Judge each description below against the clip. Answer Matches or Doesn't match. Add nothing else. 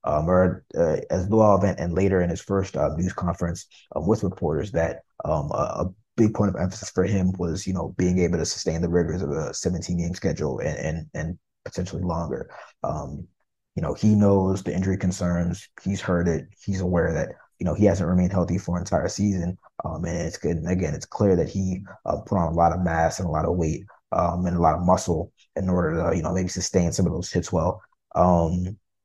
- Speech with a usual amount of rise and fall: Doesn't match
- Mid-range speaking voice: Doesn't match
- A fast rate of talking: Matches